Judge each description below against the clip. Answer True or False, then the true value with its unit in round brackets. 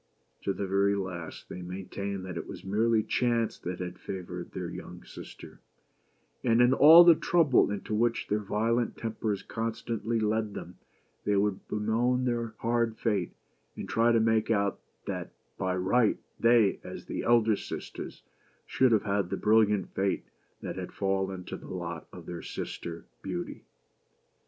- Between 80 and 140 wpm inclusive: False (160 wpm)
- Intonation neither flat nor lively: True (3.2 semitones)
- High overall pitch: False (105 Hz)